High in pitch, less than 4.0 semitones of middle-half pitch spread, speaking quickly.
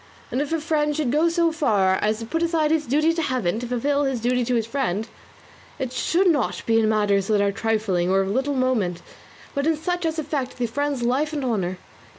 No: very high, 255 Hz; wide, 5.6 semitones; fast, 225 wpm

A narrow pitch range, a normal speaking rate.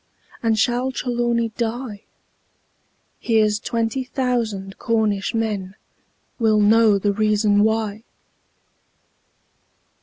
No: narrow, 2.0 semitones; slow, 85 wpm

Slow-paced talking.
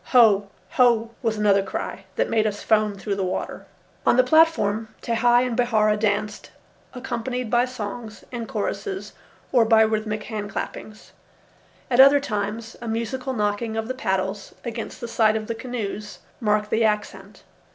No: average, 160 wpm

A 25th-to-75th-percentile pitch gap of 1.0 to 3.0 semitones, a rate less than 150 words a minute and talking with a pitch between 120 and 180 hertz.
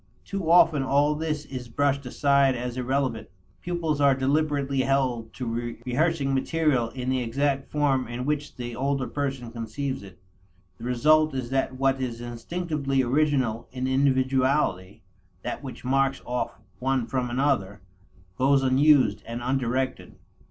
Yes: narrow, 2.4 semitones; average, 140 wpm; low, 135 Hz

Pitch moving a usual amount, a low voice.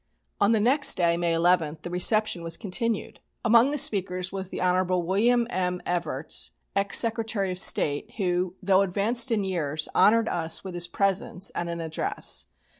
No: average, 3.6 semitones; medium, 185 Hz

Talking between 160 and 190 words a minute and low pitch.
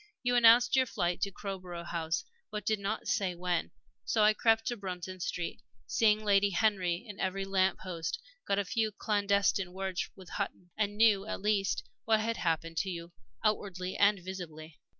No: average, 175 wpm; high, 195 Hz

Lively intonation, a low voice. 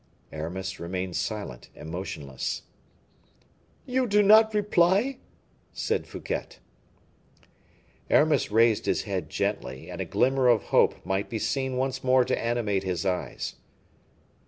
Yes: wide, 6.9 semitones; low, 110 Hz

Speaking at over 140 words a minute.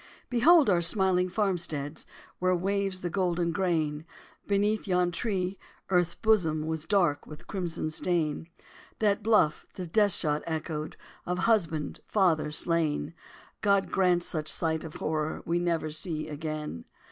No: slow, 135 wpm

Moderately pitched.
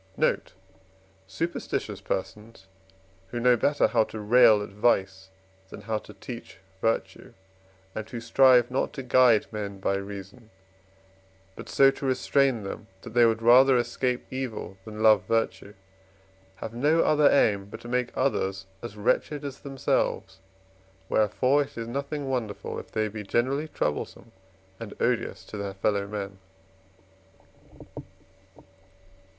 No: low, 115 Hz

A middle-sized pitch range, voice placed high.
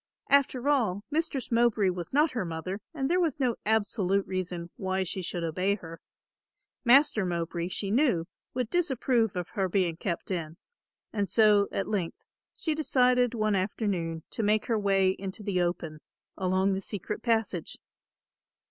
Yes: average, 4.7 semitones; high, 200 Hz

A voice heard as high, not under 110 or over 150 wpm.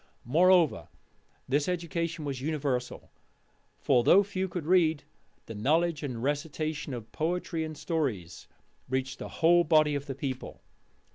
No: medium, 150 Hz; slow, 135 wpm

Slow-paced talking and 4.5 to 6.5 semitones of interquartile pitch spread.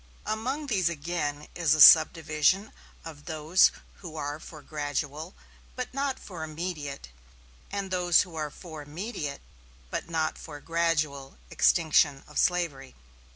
No: slow, 130 wpm; average, 3.2 semitones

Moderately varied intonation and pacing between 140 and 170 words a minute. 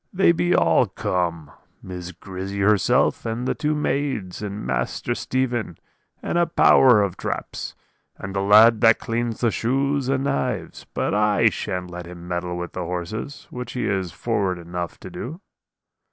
No: wide, 5.8 semitones; average, 165 wpm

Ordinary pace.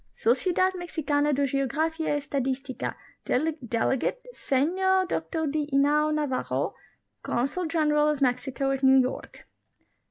No: slow, 120 wpm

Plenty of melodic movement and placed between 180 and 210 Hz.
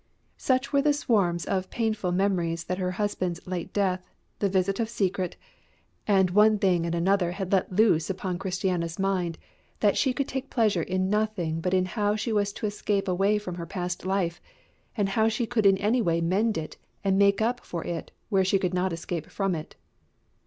No: average, 2.9 semitones; high, 190 Hz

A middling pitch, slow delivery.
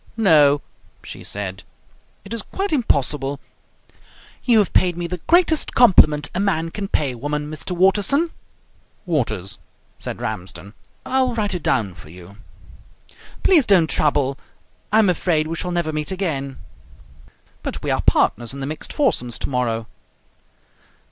No: medium, 160 Hz; average, 150 wpm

